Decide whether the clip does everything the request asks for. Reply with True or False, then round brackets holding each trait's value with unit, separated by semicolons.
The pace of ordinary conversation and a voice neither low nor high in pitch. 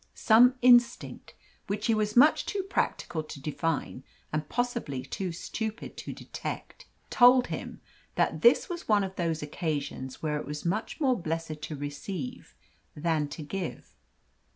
True (150 wpm; 175 Hz)